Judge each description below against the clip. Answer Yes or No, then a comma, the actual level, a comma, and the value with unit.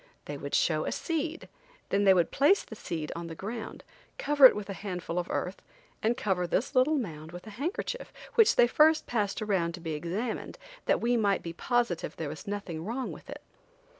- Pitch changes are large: Yes, wide, 6.6 semitones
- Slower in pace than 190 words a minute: No, fast, 205 wpm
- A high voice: Yes, high, 205 Hz